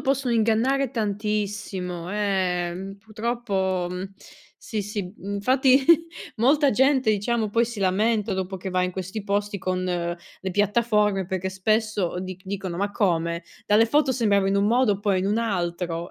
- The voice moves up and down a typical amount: Yes, average, 3.1 semitones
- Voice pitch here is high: Yes, high, 200 Hz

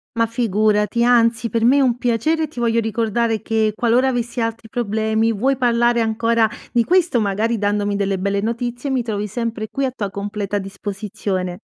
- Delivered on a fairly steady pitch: Yes, narrow, 2.3 semitones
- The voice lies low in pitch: No, high, 230 Hz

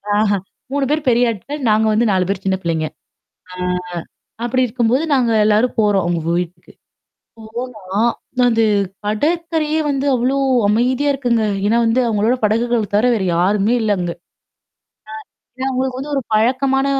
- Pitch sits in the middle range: No, high, 235 Hz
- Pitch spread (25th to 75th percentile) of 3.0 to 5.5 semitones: Yes, average, 3.9 semitones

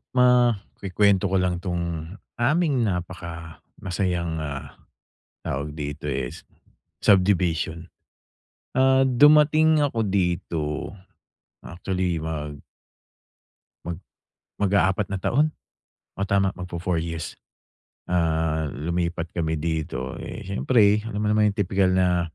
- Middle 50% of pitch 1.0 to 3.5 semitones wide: No, average, 3.9 semitones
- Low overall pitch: Yes, very low, 90 Hz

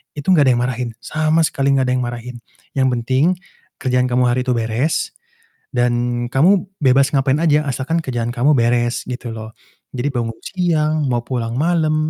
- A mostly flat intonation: No, average, 3.4 semitones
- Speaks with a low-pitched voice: Yes, low, 130 Hz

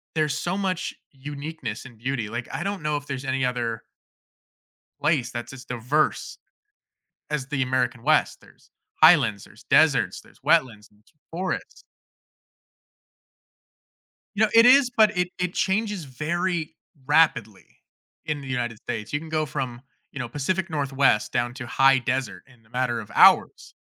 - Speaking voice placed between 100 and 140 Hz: Yes, low, 135 Hz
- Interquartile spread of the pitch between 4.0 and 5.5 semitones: Yes, average, 4.8 semitones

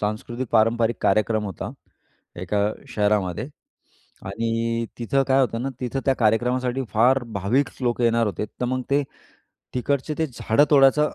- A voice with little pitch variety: No, average, 3.3 semitones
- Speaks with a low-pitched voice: Yes, low, 120 Hz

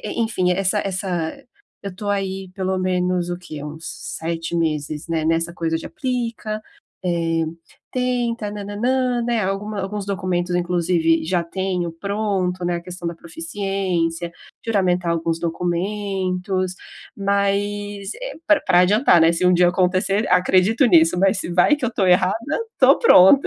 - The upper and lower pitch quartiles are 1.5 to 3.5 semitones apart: Yes, average, 3.0 semitones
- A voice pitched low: No, medium, 185 Hz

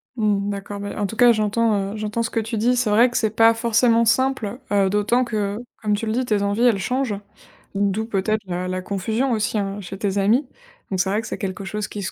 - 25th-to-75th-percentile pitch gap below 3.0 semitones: Yes, narrow, 2.4 semitones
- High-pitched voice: Yes, high, 210 Hz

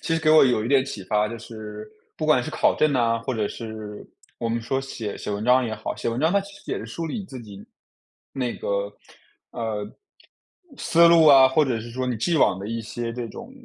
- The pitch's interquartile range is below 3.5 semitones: No, average, 4.2 semitones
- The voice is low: Yes, low, 120 Hz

